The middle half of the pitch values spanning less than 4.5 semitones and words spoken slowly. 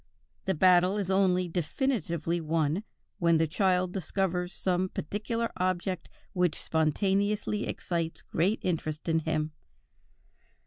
Yes: average, 2.9 semitones; slow, 115 wpm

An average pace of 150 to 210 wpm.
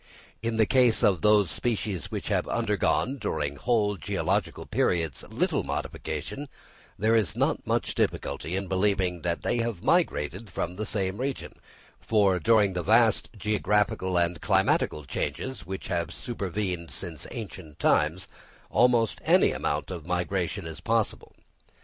No: average, 140 wpm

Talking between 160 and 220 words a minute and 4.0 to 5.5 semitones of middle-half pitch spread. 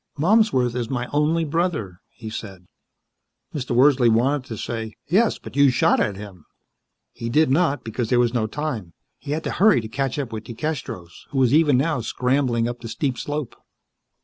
Yes: average, 185 wpm; average, 4.4 semitones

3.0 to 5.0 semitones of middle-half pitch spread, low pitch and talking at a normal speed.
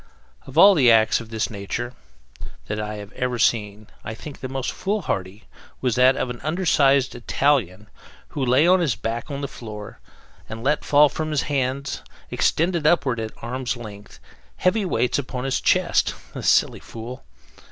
Yes: average, 4.5 semitones; low, 125 Hz; average, 175 wpm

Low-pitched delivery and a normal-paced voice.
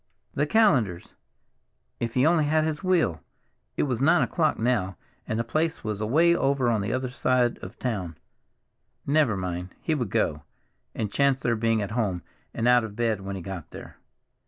Yes: low, 120 Hz; average, 180 wpm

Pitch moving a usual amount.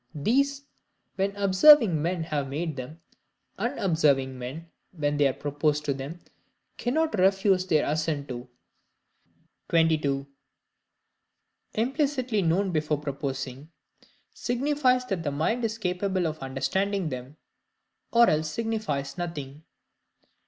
No: wide, 5.9 semitones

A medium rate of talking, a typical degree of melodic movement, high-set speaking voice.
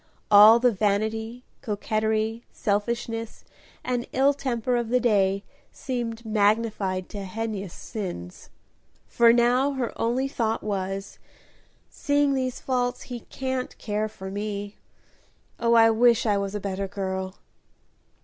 No: slow, 125 wpm; average, 3.1 semitones; high, 220 Hz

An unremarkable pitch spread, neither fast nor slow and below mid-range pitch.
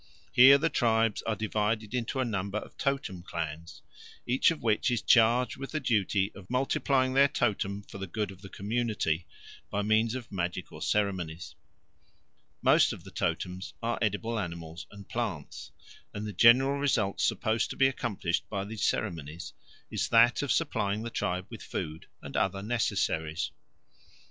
Yes: average, 4.1 semitones; average, 160 wpm; low, 105 Hz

